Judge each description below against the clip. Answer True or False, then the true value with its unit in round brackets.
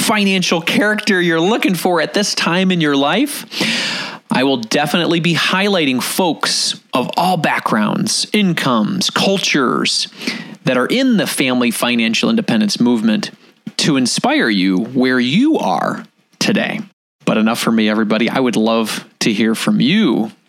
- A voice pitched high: True (200 Hz)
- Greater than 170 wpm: False (145 wpm)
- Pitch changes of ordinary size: False (7.2 semitones)